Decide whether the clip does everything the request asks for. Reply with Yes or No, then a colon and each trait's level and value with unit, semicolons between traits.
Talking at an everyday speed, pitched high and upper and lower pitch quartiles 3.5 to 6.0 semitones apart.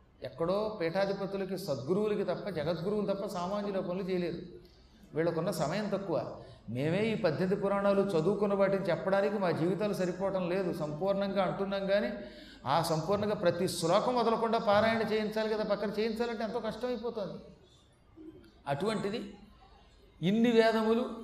No: average, 115 wpm; high, 200 Hz; average, 2.8 semitones